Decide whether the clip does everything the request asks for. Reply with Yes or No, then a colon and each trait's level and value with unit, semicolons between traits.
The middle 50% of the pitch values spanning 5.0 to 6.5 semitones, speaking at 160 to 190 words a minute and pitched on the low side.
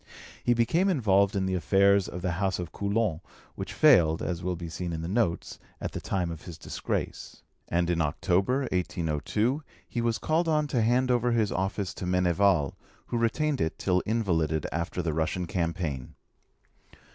Yes: average, 5.3 semitones; average, 175 wpm; very low, 95 Hz